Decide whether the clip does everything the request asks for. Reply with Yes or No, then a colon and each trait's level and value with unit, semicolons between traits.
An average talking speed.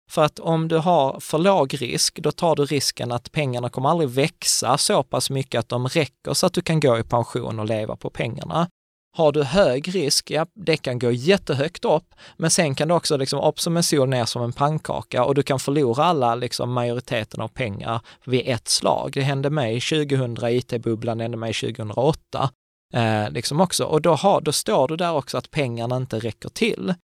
No: fast, 205 wpm